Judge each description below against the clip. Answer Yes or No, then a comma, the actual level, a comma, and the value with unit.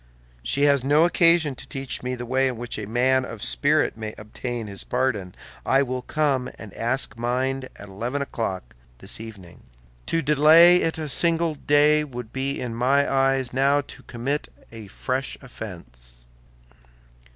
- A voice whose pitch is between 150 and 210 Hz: No, low, 130 Hz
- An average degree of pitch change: Yes, average, 3.8 semitones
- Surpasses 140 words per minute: Yes, average, 160 wpm